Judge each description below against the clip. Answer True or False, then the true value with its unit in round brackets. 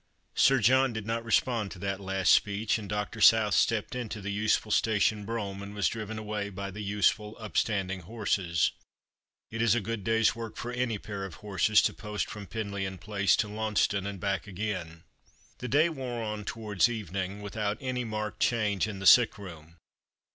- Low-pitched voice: True (105 Hz)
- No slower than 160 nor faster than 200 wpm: True (185 wpm)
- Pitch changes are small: True (2.2 semitones)